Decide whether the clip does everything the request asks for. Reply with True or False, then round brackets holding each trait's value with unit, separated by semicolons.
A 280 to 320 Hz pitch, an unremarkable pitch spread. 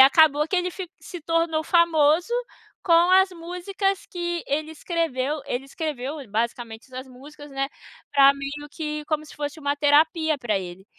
True (300 Hz; 3.5 semitones)